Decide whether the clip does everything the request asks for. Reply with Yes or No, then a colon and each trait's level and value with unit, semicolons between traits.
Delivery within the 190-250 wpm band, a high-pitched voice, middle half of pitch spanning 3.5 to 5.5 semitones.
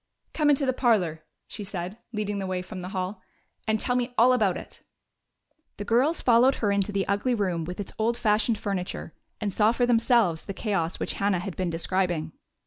Yes: average, 200 wpm; high, 205 Hz; average, 4.1 semitones